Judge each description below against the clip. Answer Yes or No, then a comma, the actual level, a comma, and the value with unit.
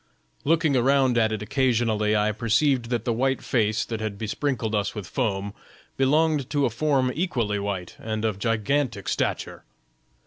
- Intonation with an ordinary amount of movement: Yes, average, 4.0 semitones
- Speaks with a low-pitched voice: Yes, low, 115 Hz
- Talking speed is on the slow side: No, average, 160 wpm